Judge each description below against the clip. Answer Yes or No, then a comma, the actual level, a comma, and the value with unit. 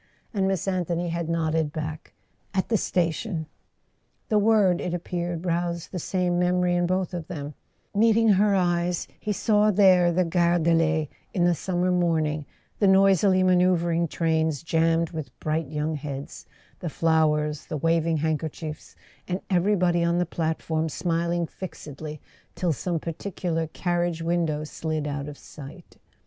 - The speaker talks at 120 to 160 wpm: Yes, average, 155 wpm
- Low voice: No, medium, 170 Hz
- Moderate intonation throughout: No, narrow, 2.2 semitones